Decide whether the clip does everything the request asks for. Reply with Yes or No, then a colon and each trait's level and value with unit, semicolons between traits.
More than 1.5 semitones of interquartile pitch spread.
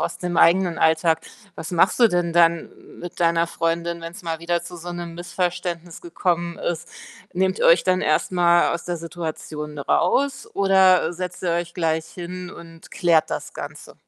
No: narrow, 1.2 semitones